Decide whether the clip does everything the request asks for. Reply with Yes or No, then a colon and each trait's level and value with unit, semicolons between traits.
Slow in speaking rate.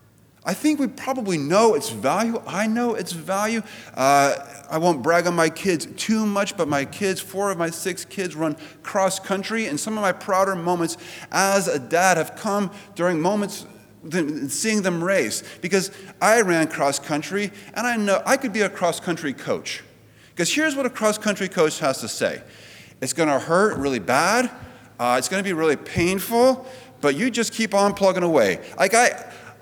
No: average, 195 wpm